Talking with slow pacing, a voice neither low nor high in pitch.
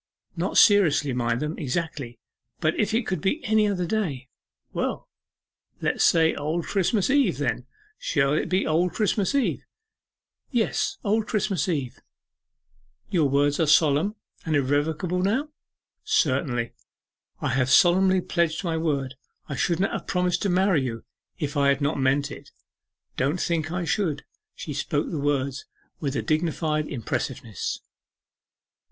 No: average, 145 wpm; medium, 160 Hz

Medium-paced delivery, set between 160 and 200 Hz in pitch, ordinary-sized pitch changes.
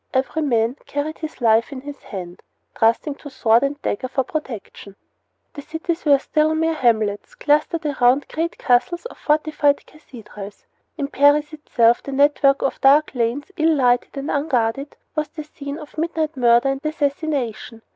No: average, 160 wpm; very high, 280 Hz; average, 4.0 semitones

